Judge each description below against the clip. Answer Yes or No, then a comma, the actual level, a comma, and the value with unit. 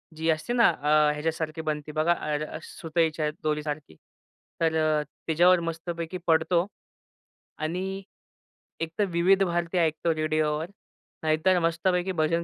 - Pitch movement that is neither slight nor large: No, narrow, 1.7 semitones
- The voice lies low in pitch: No, medium, 160 Hz